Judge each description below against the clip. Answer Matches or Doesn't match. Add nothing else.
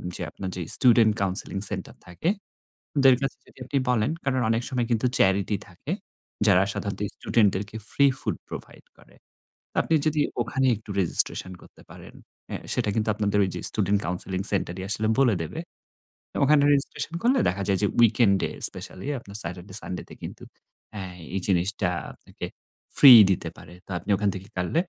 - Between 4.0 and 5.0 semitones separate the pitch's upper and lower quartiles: Matches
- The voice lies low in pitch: Matches